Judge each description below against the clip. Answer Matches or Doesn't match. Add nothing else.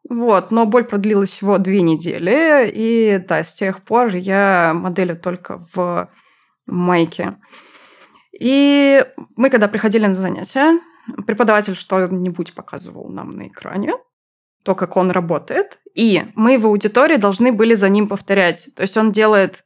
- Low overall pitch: Doesn't match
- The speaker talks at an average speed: Matches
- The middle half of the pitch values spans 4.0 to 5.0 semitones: Matches